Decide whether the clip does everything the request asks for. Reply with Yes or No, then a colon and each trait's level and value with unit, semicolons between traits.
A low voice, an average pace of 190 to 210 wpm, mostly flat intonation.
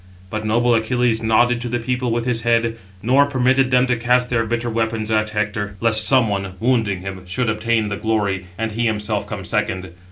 Yes: low, 115 Hz; average, 200 wpm; narrow, 2.3 semitones